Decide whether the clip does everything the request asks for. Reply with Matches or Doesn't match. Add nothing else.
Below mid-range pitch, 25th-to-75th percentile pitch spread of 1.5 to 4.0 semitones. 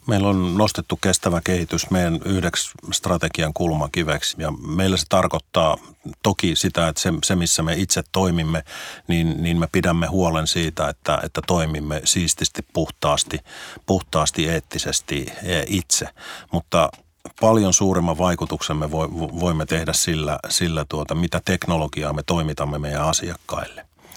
Matches